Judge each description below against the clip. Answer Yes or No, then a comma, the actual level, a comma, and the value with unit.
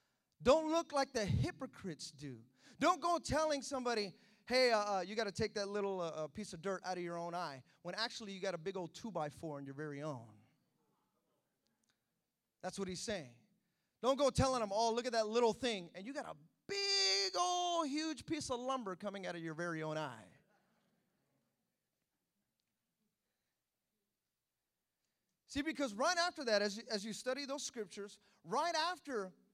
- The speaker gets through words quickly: No, average, 175 wpm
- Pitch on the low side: No, high, 205 Hz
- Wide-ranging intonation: Yes, wide, 6.4 semitones